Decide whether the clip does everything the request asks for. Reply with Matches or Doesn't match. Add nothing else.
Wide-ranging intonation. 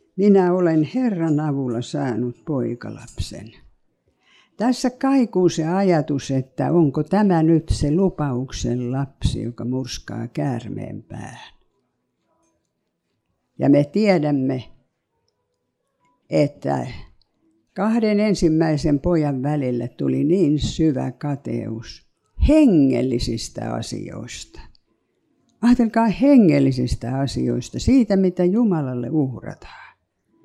Matches